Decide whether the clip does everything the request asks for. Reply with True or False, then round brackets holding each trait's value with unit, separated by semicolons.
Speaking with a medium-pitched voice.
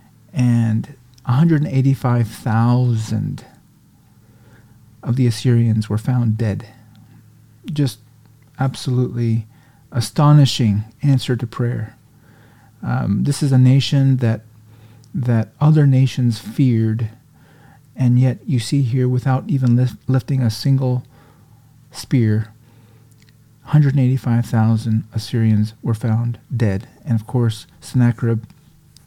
False (120 Hz)